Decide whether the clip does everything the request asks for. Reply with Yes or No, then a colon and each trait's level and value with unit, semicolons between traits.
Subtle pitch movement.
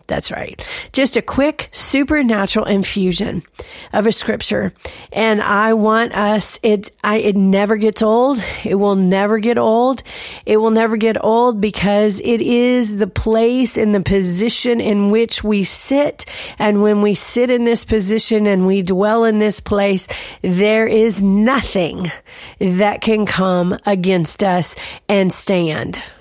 Yes: narrow, 2.2 semitones